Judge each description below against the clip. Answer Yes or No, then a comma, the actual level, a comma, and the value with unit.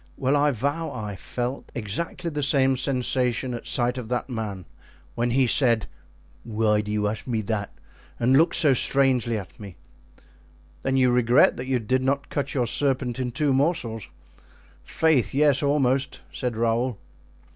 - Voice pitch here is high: No, low, 125 Hz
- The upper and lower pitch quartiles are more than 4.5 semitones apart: No, average, 3.2 semitones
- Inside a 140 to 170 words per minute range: Yes, average, 160 wpm